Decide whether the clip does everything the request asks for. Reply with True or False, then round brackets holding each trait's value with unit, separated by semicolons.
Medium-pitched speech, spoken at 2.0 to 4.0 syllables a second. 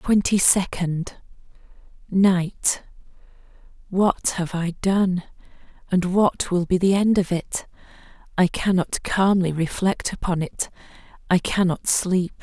True (180 Hz; 3.7 syllables/s)